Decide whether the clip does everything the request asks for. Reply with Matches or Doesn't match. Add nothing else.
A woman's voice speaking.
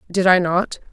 Matches